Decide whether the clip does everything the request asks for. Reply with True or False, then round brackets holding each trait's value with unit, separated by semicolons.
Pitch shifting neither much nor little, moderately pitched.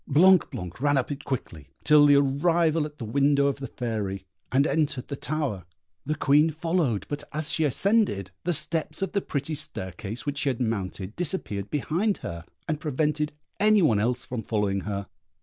False (5.7 semitones; 145 Hz)